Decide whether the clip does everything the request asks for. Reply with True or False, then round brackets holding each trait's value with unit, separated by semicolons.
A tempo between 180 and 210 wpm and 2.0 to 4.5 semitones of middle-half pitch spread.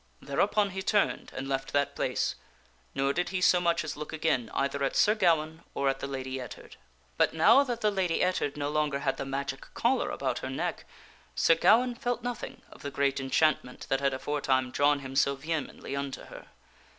False (200 wpm; 5.1 semitones)